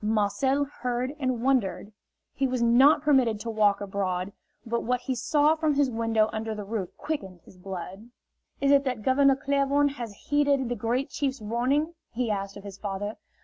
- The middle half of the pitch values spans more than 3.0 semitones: Yes, average, 4.9 semitones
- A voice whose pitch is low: No, high, 240 Hz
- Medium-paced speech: Yes, average, 180 wpm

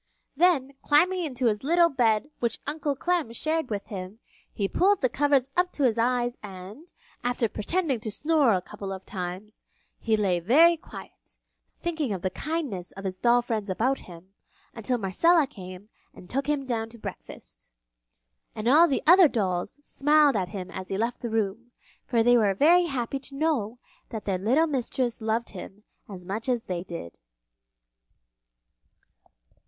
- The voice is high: Yes, high, 235 Hz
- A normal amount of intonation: No, wide, 6.4 semitones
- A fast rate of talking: No, average, 170 wpm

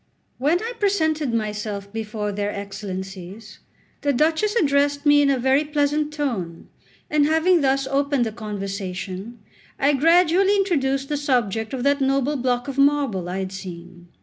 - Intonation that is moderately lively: No, wide, 6.1 semitones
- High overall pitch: Yes, very high, 270 Hz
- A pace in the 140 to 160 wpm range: Yes, average, 150 wpm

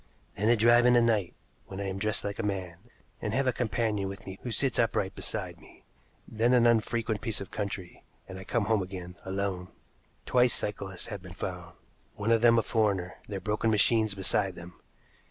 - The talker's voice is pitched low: Yes, low, 105 Hz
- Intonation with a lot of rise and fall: No, average, 3.3 semitones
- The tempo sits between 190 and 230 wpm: Yes, average, 200 wpm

